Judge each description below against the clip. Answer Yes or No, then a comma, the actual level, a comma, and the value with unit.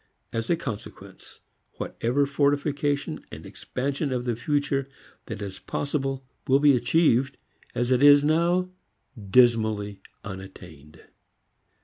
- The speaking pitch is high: No, low, 135 Hz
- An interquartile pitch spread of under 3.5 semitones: No, average, 4.2 semitones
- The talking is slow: Yes, slow, 110 wpm